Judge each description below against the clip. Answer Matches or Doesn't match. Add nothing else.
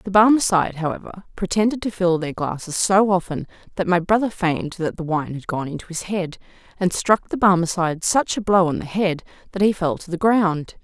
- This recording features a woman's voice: Matches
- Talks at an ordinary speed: Doesn't match